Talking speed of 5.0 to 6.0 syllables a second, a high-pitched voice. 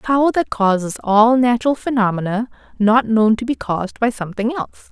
Yes: 5.9 syllables/s; high, 230 Hz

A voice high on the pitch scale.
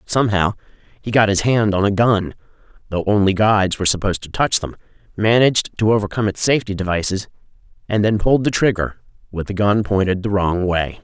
No: low, 100 Hz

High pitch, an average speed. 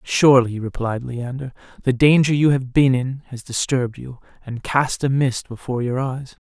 No: low, 130 Hz; average, 175 wpm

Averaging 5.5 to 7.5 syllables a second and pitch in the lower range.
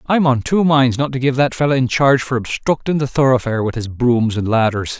Yes: 5.8 syllables/s; low, 130 Hz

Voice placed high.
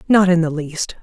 No: medium, 170 Hz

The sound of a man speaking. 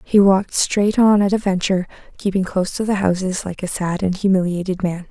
No: female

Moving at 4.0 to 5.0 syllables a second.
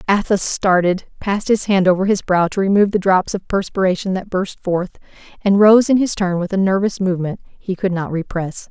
No: 5.4 syllables/s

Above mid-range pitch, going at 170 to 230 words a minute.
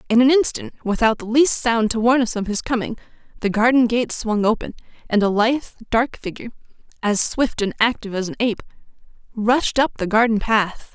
Yes: high, 230 Hz; average, 190 wpm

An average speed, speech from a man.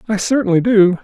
Yes: average, 175 wpm; male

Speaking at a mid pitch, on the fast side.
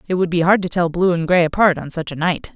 Yes: medium, 175 Hz; fast, 330 wpm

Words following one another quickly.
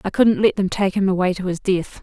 Yes: fast, 295 wpm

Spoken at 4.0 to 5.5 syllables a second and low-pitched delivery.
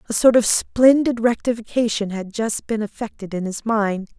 No: 4.8 syllables/s; high, 220 Hz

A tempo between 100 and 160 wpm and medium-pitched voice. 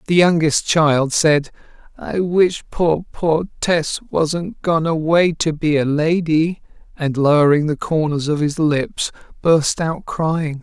Yes: average, 145 wpm; medium, 155 Hz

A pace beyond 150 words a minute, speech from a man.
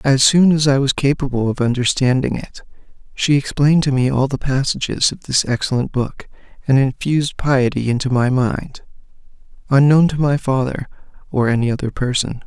Yes: average, 165 wpm; male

